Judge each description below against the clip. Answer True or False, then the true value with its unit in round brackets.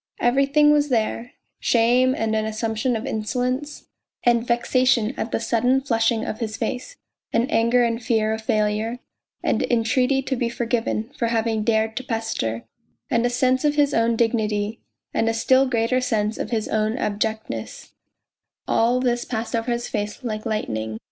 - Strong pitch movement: False (2.4 semitones)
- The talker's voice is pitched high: True (230 Hz)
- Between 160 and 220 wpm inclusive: True (170 wpm)